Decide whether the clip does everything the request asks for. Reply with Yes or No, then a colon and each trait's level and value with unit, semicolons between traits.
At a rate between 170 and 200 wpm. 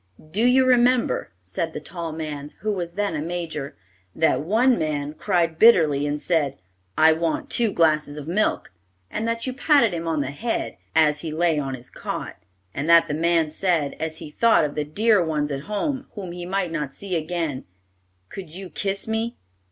Yes: average, 190 wpm